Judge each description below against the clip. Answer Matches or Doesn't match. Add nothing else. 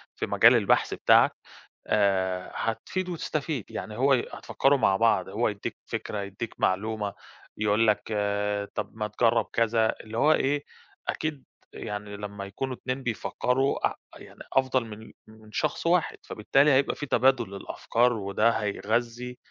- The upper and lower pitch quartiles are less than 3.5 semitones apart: Doesn't match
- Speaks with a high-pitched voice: Doesn't match